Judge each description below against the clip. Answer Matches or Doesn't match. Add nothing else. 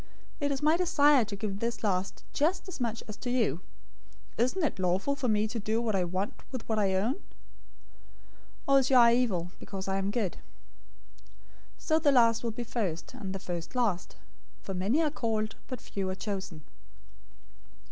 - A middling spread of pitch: Matches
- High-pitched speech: Matches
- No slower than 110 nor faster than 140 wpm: Doesn't match